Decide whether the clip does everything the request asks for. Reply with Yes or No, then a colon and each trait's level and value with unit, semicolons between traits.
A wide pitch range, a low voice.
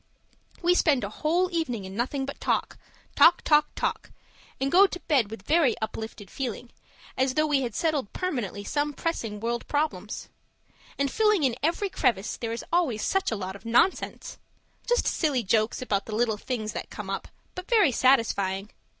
No: wide, 6.5 semitones; very high, 260 Hz